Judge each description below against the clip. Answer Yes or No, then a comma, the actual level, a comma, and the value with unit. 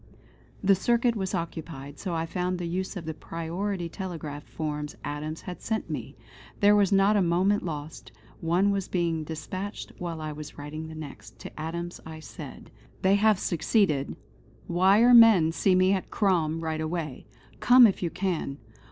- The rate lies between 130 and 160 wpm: No, average, 170 wpm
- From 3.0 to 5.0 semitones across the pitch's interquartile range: Yes, average, 3.7 semitones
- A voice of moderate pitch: Yes, medium, 175 Hz